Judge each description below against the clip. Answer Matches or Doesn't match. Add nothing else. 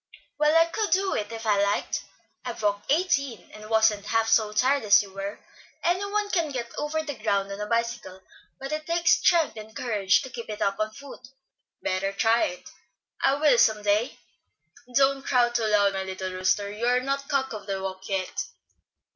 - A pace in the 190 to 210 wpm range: Matches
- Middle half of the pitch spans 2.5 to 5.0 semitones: Doesn't match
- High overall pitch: Matches